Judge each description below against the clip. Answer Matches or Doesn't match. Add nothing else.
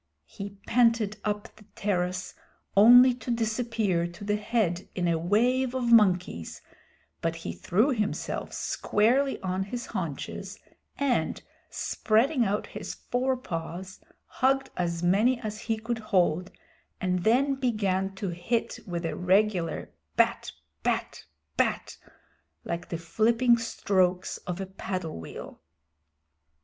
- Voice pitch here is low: Doesn't match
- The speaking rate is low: Matches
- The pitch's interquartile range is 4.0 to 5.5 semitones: Matches